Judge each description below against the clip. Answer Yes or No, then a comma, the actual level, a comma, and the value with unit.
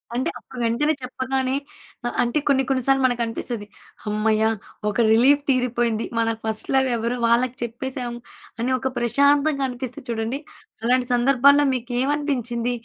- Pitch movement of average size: No, narrow, 2.3 semitones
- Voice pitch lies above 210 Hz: Yes, very high, 250 Hz